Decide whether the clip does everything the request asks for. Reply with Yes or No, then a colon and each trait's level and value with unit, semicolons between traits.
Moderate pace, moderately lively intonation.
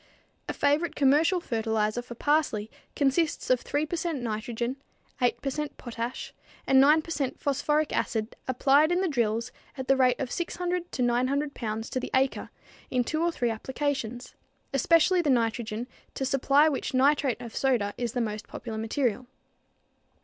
Yes: average, 165 wpm; average, 3.9 semitones